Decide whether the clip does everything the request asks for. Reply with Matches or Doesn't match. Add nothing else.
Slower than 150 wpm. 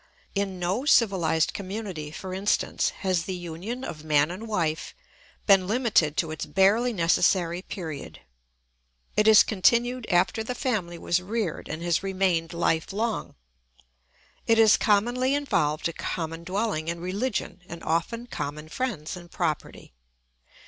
Matches